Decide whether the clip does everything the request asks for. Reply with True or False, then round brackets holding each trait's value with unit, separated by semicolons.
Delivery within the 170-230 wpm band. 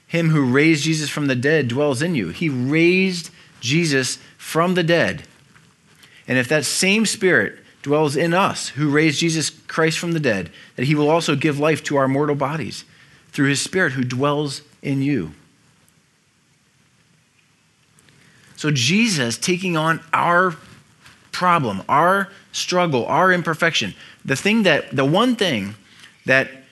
False (145 wpm)